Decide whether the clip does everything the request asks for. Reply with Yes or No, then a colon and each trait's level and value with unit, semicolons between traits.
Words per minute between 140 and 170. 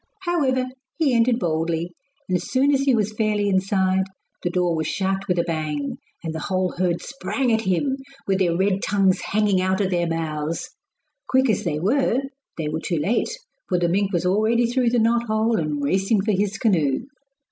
No: average, 195 wpm